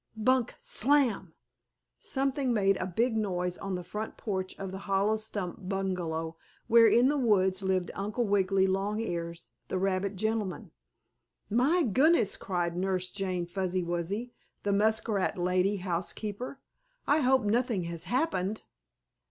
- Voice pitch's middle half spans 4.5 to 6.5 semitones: No, average, 3.6 semitones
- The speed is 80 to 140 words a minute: Yes, slow, 135 wpm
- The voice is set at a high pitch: Yes, high, 195 Hz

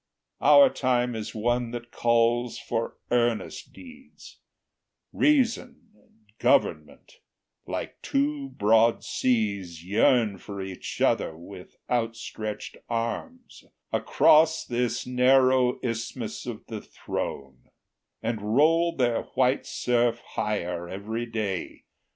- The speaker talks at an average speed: No, slow, 105 wpm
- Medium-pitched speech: No, low, 115 Hz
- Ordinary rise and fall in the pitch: Yes, average, 3.3 semitones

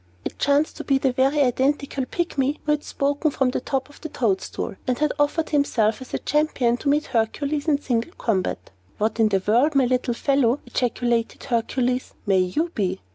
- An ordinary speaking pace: Yes, average, 190 wpm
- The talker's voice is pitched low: No, very high, 265 Hz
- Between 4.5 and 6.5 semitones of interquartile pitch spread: No, average, 3.6 semitones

